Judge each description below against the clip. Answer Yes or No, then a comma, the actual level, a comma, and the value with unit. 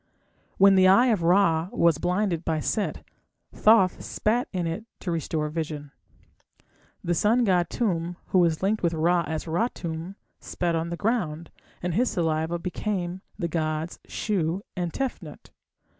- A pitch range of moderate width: Yes, average, 3.3 semitones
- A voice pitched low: No, medium, 175 Hz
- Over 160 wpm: No, average, 155 wpm